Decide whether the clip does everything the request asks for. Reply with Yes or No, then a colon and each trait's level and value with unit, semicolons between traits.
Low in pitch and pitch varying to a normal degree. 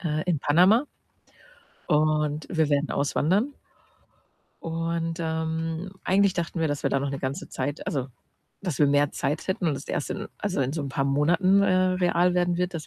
No: medium, 160 Hz; average, 3.6 semitones